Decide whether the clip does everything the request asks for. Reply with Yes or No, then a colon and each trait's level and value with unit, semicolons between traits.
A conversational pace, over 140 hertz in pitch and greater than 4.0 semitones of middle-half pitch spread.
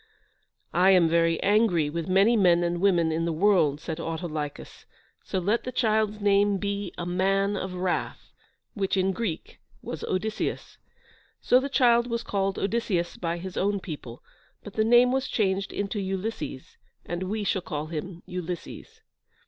No: average, 160 wpm; high, 190 Hz; average, 3.3 semitones